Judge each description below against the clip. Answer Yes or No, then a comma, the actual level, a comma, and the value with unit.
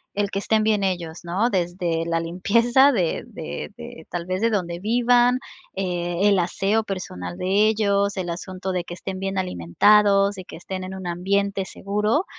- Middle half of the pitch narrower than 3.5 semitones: Yes, average, 2.9 semitones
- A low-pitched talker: No, high, 190 Hz